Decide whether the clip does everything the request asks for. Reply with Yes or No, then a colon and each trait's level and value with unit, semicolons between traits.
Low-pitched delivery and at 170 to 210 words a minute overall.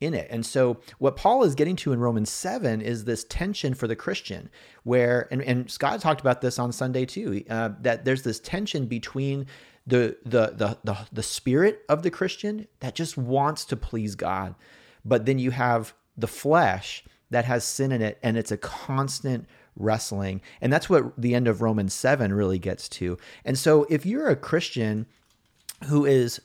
Yes: low, 125 Hz; average, 190 wpm